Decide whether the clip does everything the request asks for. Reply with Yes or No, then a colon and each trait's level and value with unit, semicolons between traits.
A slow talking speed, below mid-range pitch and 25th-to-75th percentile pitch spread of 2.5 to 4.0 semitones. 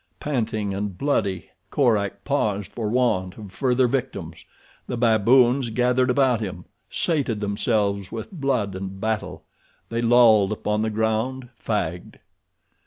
Yes: slow, 125 wpm; low, 110 Hz; average, 3.7 semitones